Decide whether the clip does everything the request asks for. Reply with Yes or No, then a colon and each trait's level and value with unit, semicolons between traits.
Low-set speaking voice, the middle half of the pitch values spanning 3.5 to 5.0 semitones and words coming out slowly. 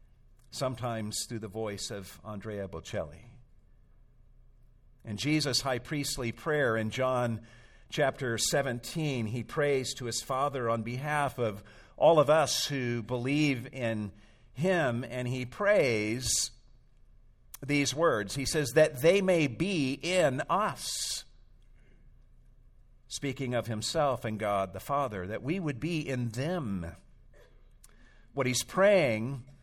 Yes: low, 125 Hz; average, 4.3 semitones; slow, 120 wpm